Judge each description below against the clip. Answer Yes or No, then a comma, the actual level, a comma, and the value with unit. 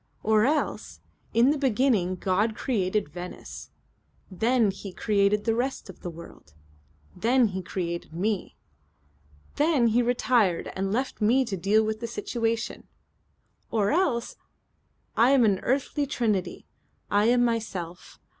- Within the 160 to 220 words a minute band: No, slow, 135 wpm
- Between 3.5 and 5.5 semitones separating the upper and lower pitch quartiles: Yes, average, 4.1 semitones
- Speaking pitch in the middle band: No, high, 220 Hz